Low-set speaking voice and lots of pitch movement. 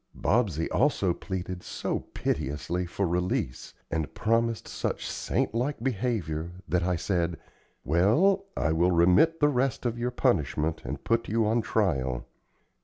Yes: very low, 95 Hz; wide, 5.8 semitones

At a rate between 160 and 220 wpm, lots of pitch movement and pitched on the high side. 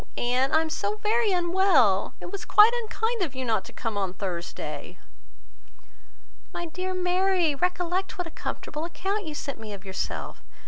Yes: average, 170 wpm; wide, 7.8 semitones; very high, 340 Hz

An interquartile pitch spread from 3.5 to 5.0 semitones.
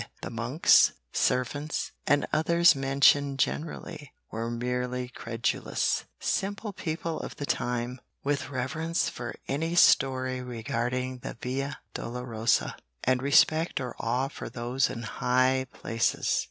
No: average, 2.7 semitones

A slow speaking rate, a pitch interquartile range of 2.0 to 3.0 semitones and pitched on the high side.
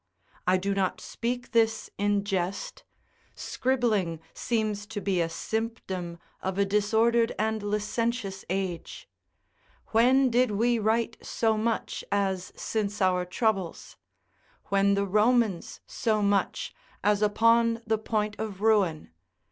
Yes: slow, 125 wpm; average, 2.7 semitones; high, 210 Hz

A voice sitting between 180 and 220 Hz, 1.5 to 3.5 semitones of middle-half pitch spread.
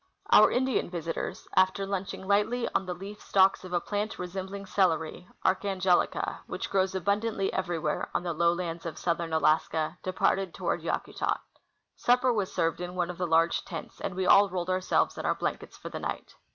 Yes: medium, 185 Hz; narrow, 2.5 semitones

